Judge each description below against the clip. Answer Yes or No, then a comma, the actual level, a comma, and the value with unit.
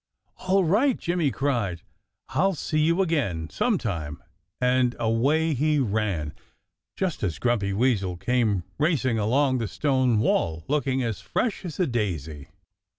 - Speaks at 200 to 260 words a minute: No, slow, 135 wpm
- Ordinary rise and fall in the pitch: No, wide, 7.3 semitones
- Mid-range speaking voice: No, low, 125 Hz